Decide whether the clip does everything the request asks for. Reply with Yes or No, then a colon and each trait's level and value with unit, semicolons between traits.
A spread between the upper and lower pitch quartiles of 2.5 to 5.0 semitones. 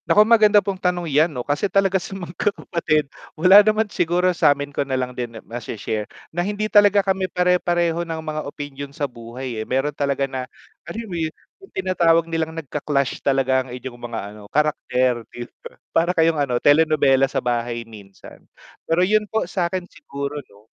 No: wide, 5.5 semitones